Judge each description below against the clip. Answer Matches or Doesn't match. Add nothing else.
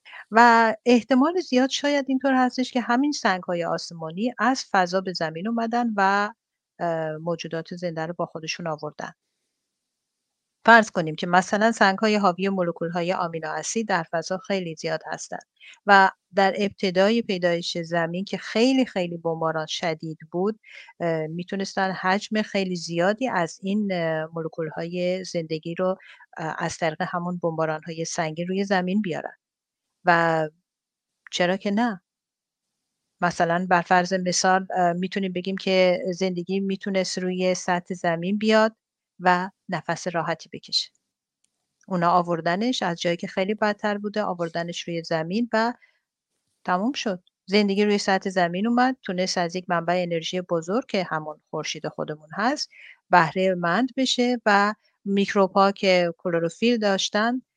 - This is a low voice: Doesn't match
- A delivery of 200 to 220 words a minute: Doesn't match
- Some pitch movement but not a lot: Matches